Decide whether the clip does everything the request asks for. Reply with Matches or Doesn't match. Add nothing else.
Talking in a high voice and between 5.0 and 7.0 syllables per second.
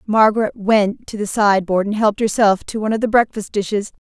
Matches